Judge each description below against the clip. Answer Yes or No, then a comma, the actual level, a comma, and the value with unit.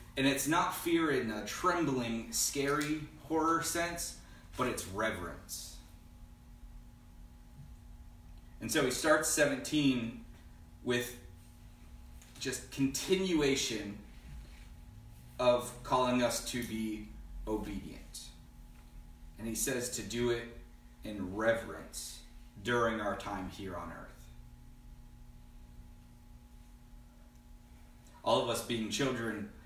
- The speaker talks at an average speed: No, slow, 95 wpm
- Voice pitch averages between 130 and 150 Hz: No, low, 110 Hz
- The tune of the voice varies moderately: No, wide, 7.4 semitones